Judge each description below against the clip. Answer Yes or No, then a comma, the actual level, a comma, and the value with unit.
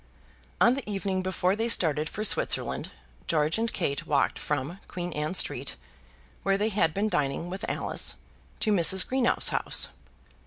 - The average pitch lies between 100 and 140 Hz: No, medium, 185 Hz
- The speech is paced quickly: No, average, 155 wpm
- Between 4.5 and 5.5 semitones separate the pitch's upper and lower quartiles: Yes, average, 5.1 semitones